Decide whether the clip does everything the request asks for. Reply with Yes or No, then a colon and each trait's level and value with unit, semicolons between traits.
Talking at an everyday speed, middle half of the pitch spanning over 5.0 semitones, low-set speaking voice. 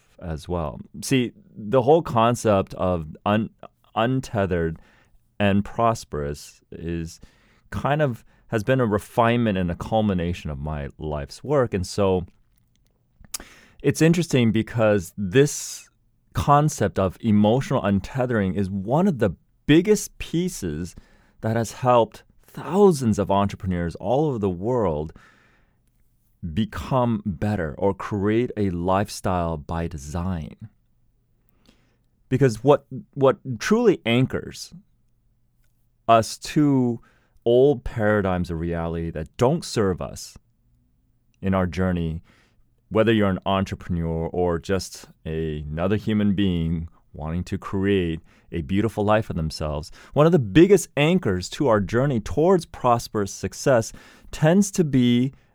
No: slow, 120 wpm; wide, 5.4 semitones; low, 105 Hz